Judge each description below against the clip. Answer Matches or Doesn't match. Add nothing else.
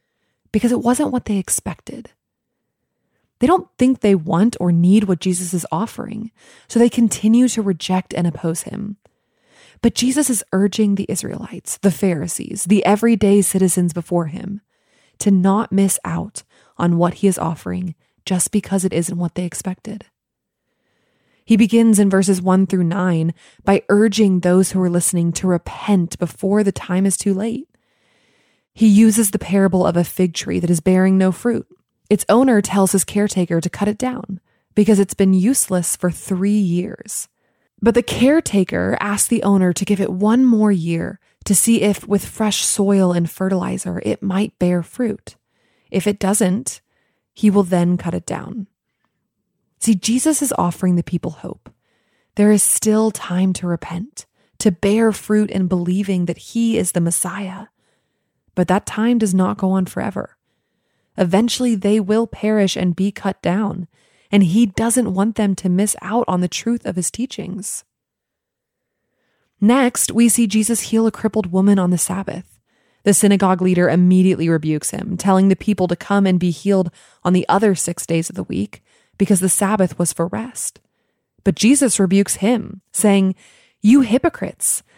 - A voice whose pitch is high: Matches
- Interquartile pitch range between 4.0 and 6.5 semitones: Doesn't match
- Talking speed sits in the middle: Matches